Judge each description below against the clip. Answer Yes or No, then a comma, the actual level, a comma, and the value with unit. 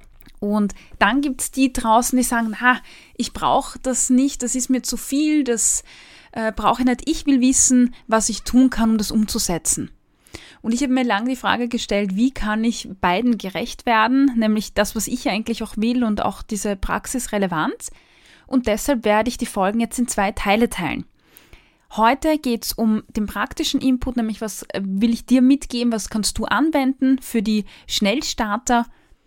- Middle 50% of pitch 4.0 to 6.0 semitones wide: No, average, 3.1 semitones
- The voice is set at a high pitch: Yes, high, 235 Hz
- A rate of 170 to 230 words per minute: Yes, average, 185 wpm